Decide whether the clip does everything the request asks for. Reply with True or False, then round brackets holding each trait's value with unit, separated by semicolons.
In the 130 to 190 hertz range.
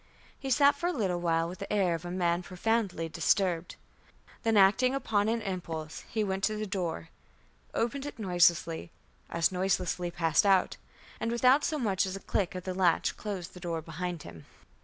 True (185 Hz)